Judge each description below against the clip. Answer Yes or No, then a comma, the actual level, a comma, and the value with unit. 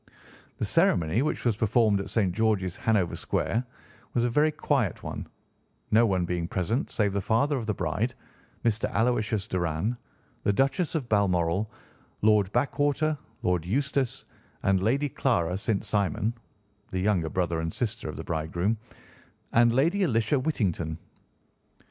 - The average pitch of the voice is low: Yes, low, 105 Hz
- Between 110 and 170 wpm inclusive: Yes, average, 145 wpm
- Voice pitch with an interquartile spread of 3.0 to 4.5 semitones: No, average, 5.0 semitones